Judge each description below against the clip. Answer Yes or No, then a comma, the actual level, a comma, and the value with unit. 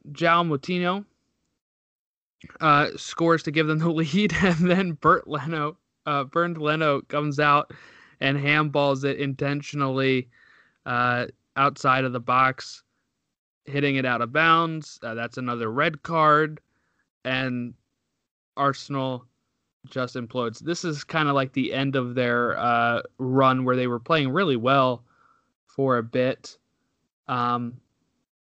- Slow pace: Yes, slow, 130 wpm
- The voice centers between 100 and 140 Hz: Yes, low, 135 Hz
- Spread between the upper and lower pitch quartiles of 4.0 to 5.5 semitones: No, average, 3.5 semitones